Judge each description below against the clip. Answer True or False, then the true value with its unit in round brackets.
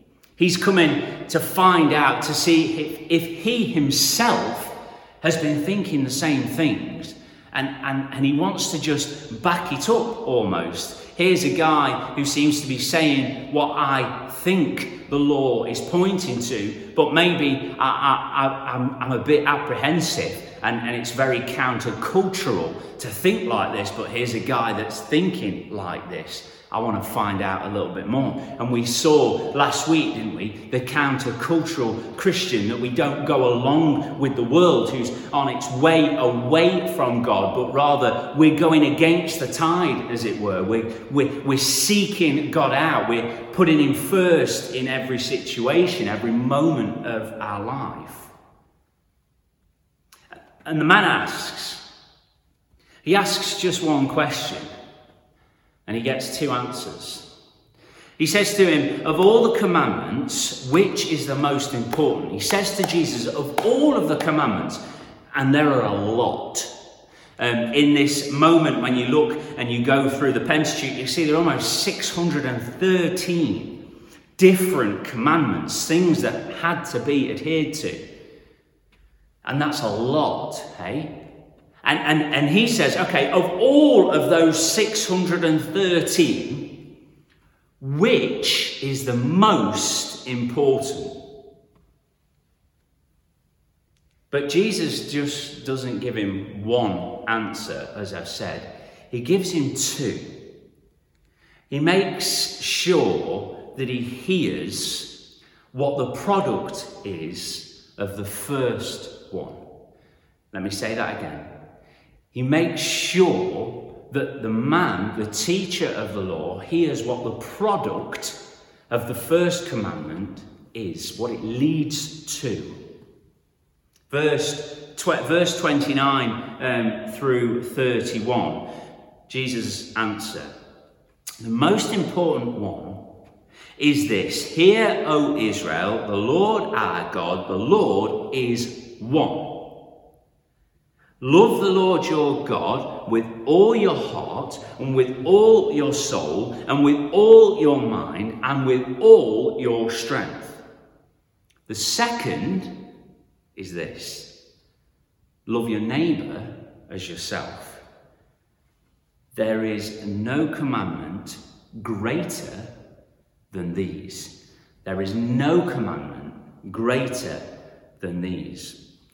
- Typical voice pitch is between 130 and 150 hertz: True (140 Hz)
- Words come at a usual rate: False (125 wpm)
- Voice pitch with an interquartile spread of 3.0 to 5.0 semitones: False (5.4 semitones)